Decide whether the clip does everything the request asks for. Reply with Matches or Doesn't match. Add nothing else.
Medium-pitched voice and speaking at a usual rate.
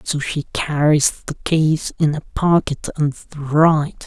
Matches